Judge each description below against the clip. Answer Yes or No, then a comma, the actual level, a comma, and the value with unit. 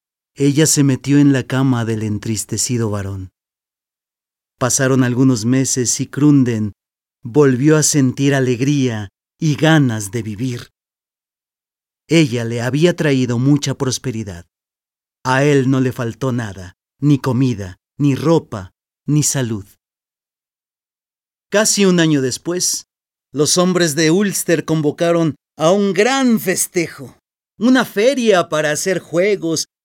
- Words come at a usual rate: No, slow, 115 wpm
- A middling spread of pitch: Yes, average, 4.6 semitones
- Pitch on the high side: No, low, 135 Hz